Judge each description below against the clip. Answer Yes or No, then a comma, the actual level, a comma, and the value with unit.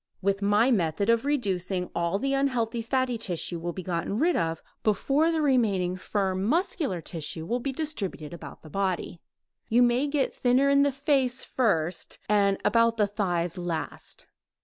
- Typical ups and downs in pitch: No, wide, 6.4 semitones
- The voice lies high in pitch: Yes, high, 210 Hz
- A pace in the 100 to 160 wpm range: No, average, 170 wpm